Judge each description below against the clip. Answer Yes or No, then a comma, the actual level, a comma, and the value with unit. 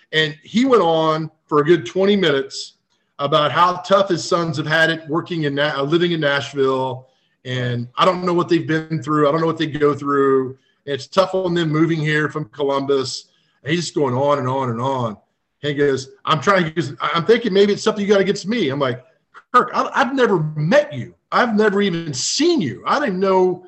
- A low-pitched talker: No, medium, 160 Hz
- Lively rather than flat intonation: No, average, 4.7 semitones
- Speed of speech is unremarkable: No, fast, 215 wpm